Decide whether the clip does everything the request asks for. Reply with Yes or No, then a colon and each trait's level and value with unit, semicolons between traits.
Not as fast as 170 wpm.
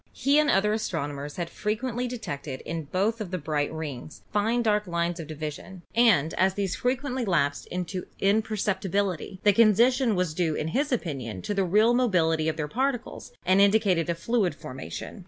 No: average, 175 wpm